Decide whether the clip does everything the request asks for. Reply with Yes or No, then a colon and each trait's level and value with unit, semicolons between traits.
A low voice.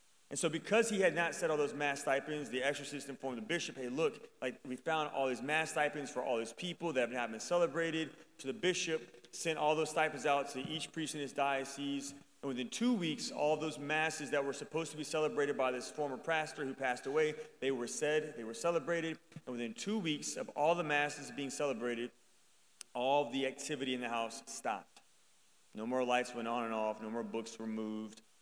No: medium, 145 Hz